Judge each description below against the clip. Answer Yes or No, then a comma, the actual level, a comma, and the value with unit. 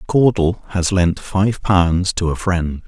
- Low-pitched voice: Yes, very low, 90 Hz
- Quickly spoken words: No, average, 165 wpm